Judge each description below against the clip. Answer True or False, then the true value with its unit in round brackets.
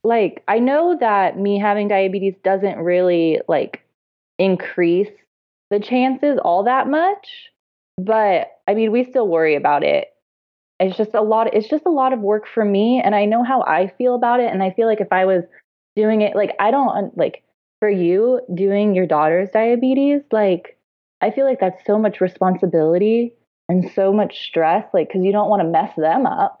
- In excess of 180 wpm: True (190 wpm)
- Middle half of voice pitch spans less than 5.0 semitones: True (4.5 semitones)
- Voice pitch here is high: True (205 Hz)